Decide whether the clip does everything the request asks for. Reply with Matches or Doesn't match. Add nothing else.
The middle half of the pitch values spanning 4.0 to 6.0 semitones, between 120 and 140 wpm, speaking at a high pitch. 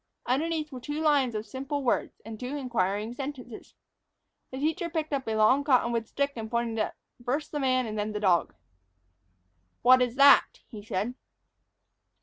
Doesn't match